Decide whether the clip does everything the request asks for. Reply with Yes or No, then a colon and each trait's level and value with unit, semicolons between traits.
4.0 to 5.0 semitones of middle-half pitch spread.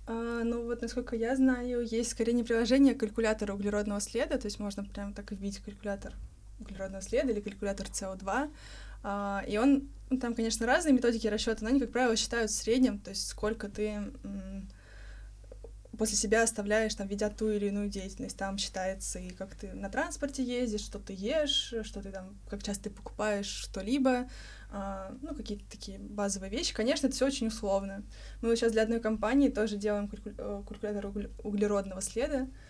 No: average, 2.8 semitones